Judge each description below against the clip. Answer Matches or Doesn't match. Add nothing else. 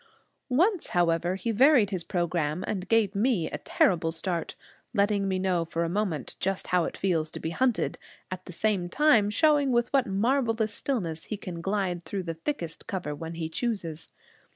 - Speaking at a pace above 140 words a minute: Matches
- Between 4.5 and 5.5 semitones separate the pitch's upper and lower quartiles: Matches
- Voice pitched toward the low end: Doesn't match